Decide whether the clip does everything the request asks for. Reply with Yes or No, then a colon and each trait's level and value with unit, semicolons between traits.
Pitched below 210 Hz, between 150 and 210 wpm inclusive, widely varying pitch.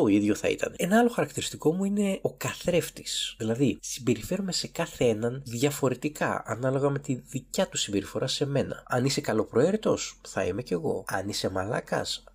Yes: medium, 140 Hz; fast, 170 wpm; wide, 6.1 semitones